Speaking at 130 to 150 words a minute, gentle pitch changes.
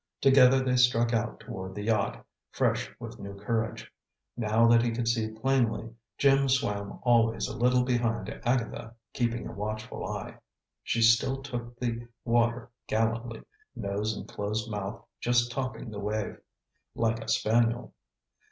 Yes: average, 145 wpm; narrow, 1.9 semitones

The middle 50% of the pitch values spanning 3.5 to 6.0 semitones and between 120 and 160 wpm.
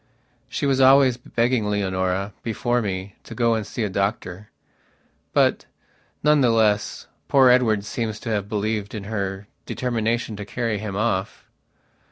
No: average, 3.0 semitones; average, 150 wpm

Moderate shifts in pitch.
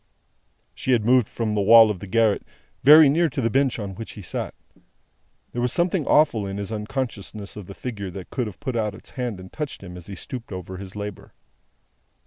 Yes: average, 4.3 semitones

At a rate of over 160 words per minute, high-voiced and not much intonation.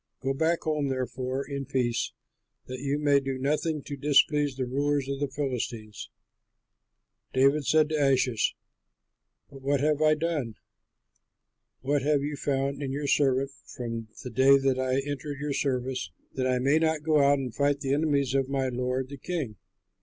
No: average, 170 wpm; medium, 140 Hz; narrow, 2.0 semitones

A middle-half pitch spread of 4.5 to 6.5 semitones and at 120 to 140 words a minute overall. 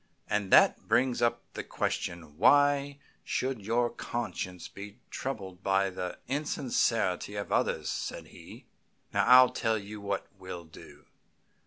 Yes: average, 5.0 semitones; slow, 135 wpm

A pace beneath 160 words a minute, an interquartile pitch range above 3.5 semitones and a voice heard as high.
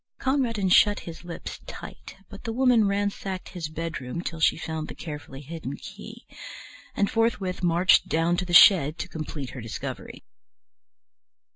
No: average, 150 wpm; average, 4.2 semitones; medium, 175 Hz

